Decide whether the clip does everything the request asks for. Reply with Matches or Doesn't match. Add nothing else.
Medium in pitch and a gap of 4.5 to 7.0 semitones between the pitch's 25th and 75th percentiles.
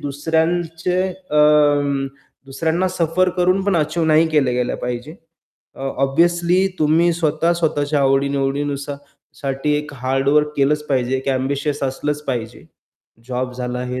Doesn't match